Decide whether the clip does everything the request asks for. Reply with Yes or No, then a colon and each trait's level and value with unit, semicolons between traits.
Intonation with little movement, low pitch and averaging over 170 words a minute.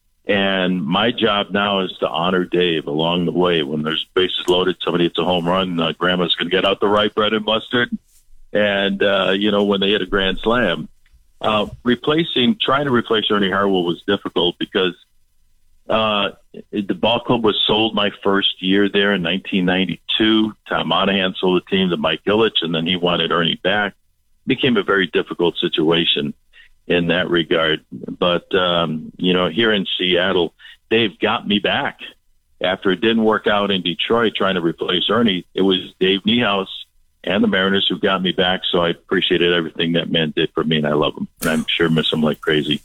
No: average, 3.2 semitones; very low, 95 Hz; average, 195 wpm